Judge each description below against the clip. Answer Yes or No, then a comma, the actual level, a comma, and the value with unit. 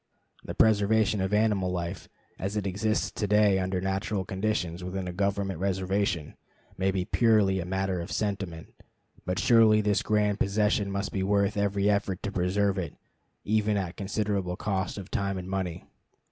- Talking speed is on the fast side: No, average, 165 wpm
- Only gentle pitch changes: Yes, narrow, 1.8 semitones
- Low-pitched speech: Yes, low, 100 Hz